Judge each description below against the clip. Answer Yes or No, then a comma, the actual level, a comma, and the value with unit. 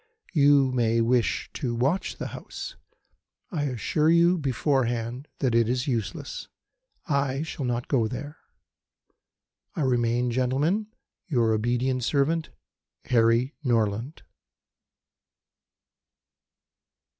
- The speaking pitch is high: No, low, 130 Hz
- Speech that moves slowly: Yes, slow, 100 wpm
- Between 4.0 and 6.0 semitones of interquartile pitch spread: No, average, 3.5 semitones